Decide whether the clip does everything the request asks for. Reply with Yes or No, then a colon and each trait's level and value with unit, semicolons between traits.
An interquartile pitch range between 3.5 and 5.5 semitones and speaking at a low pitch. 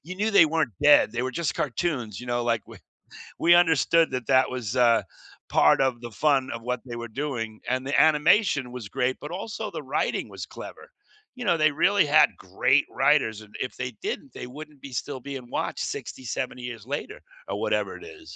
Yes: average, 4.4 semitones; low, 130 Hz